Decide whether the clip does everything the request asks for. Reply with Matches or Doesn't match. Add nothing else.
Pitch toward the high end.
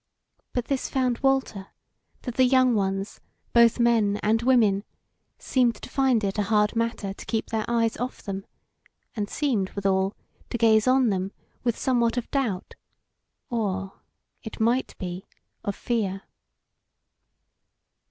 Matches